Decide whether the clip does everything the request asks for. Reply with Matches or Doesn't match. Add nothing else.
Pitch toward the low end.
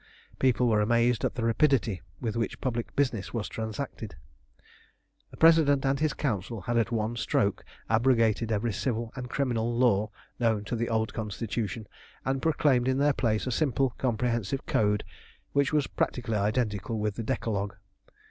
Matches